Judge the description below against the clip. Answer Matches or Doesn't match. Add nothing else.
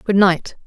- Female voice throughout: Matches